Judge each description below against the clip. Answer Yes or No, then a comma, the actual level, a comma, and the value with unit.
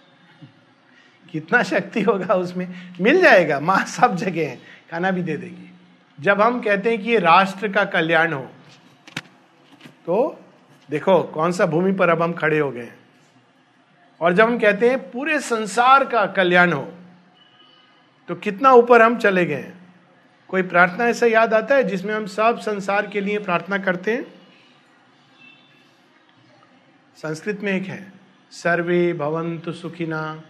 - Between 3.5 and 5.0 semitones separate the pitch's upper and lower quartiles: Yes, average, 4.3 semitones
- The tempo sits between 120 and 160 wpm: Yes, average, 140 wpm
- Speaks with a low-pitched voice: No, high, 190 Hz